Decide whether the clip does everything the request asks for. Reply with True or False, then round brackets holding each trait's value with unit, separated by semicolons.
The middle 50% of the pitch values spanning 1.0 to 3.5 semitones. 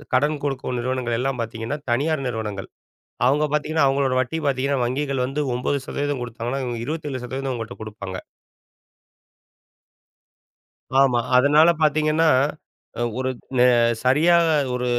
True (3.1 semitones)